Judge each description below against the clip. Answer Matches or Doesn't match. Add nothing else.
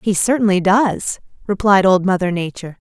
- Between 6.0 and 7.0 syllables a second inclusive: Doesn't match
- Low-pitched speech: Doesn't match